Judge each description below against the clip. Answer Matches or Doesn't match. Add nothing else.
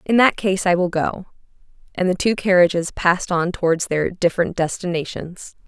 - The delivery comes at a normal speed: Matches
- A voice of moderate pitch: Matches